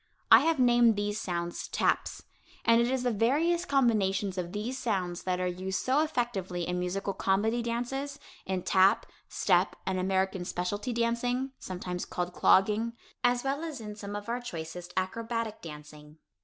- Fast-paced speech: No, average, 160 wpm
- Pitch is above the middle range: Yes, high, 210 Hz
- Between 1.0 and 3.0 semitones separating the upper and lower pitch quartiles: No, average, 4.8 semitones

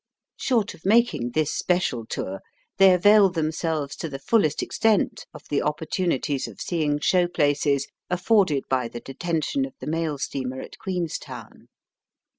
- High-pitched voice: No, medium, 160 Hz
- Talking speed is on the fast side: No, average, 150 wpm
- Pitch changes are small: No, average, 4.7 semitones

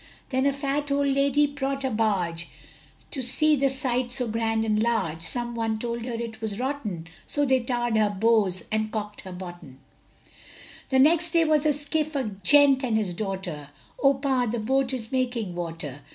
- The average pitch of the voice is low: No, high, 240 Hz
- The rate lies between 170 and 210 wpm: Yes, average, 180 wpm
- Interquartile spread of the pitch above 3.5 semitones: Yes, average, 4.5 semitones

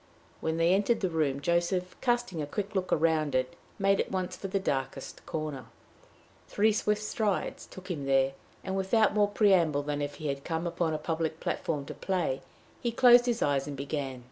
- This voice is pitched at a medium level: Yes, medium, 170 Hz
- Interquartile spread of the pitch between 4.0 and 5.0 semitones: No, wide, 5.4 semitones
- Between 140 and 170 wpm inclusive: No, average, 195 wpm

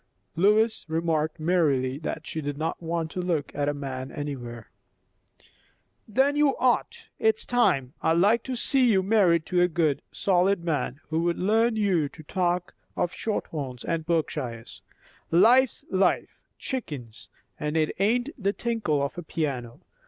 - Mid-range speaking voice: Yes, medium, 170 Hz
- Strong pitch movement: Yes, wide, 5.8 semitones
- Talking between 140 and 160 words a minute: Yes, average, 150 wpm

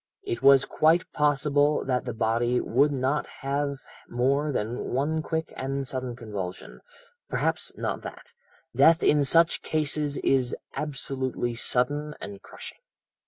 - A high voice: No, medium, 140 Hz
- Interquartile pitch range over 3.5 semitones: No, average, 3.2 semitones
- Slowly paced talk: Yes, slow, 130 wpm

